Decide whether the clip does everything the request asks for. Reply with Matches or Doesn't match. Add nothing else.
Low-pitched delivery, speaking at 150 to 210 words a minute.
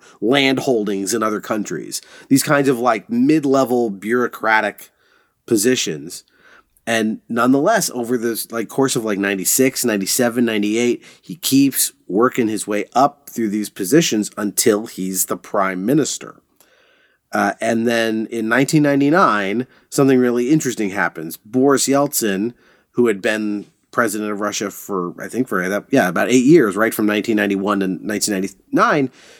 Doesn't match